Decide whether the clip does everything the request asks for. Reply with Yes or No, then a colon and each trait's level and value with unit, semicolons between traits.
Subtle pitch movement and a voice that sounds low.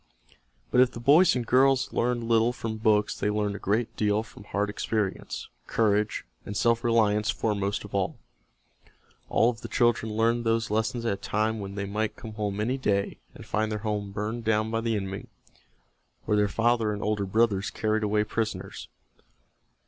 Yes: narrow, 2.0 semitones; low, 110 Hz